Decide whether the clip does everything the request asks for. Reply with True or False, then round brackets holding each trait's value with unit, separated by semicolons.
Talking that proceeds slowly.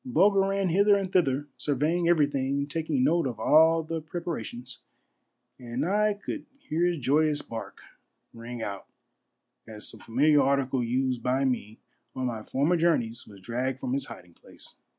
False (155 wpm)